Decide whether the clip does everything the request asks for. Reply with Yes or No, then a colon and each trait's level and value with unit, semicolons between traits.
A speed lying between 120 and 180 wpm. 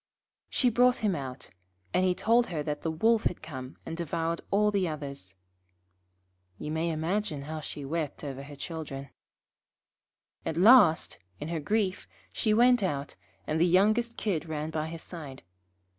Yes: average, 160 wpm